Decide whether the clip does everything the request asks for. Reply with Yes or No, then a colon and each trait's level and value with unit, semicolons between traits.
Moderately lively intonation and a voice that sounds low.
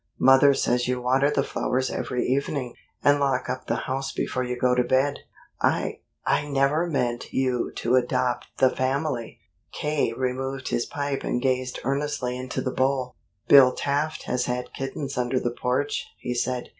No: narrow, 1.8 semitones; low, 130 Hz